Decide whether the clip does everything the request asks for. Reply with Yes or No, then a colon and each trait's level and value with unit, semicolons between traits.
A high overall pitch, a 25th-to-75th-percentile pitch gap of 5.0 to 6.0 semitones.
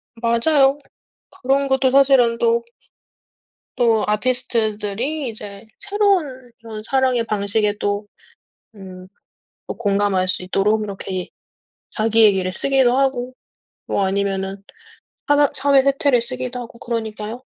No: high, 230 Hz; average, 4.3 semitones